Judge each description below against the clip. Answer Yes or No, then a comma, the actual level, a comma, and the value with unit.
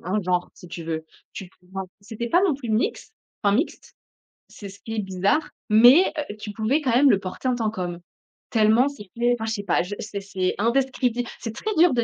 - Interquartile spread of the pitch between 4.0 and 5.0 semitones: Yes, average, 4.3 semitones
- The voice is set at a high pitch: Yes, high, 220 Hz